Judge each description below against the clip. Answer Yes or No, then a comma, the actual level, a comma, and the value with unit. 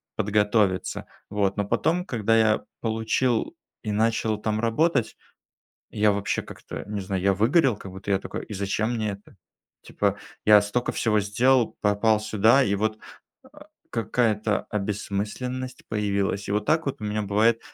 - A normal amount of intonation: No, narrow, 2.0 semitones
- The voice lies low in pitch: Yes, low, 105 Hz